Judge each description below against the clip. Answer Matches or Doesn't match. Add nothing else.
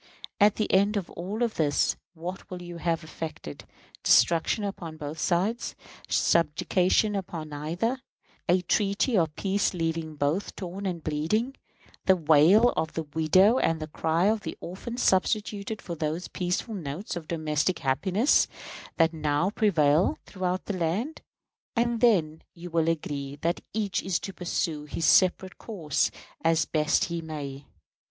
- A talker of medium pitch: Matches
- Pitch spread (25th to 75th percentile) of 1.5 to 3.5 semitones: Doesn't match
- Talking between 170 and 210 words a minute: Doesn't match